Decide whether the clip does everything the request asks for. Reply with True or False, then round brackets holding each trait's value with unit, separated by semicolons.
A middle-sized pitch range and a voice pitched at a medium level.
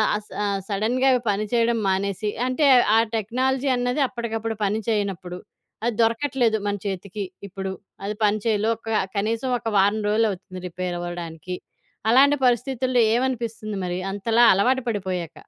False (3.6 semitones; 220 Hz)